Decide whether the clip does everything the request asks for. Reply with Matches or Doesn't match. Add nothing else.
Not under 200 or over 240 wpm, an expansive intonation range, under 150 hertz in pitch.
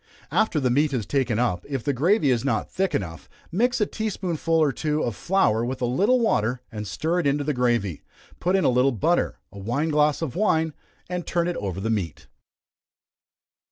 Matches